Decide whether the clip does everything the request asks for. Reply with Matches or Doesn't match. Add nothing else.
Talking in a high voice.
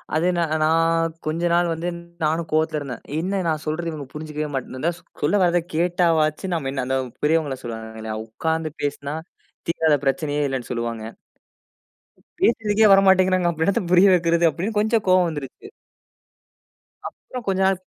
Doesn't match